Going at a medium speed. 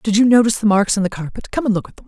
No: fast, 345 wpm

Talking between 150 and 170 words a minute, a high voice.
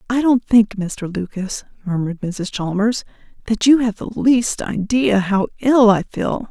Yes: average, 165 wpm; high, 215 Hz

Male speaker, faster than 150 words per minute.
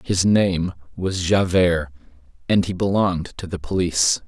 No: male; average, 140 wpm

